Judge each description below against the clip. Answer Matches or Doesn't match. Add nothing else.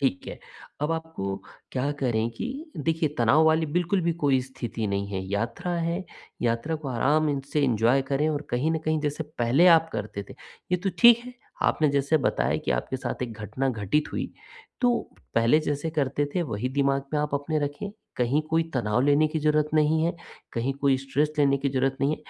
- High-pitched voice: Doesn't match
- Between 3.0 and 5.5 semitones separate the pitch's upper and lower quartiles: Matches